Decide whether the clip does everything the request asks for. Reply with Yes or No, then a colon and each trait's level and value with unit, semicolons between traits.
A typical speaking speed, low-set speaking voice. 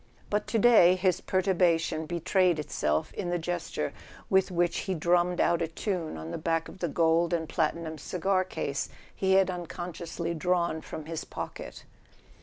No: average, 175 wpm; medium, 175 Hz